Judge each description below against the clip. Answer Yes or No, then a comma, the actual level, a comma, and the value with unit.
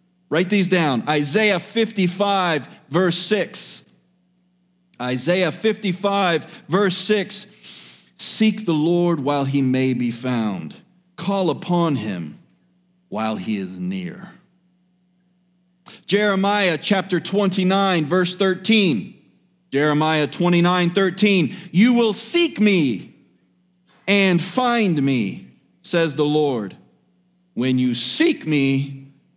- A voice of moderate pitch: Yes, medium, 180 Hz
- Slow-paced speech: Yes, slow, 100 wpm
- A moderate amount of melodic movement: Yes, average, 3.9 semitones